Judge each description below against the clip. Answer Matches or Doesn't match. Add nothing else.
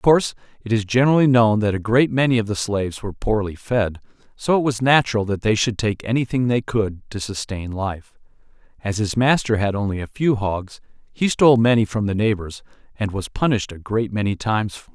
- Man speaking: Matches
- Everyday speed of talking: Doesn't match